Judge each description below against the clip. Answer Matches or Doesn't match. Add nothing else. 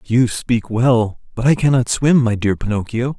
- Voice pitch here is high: Doesn't match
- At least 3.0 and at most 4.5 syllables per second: Matches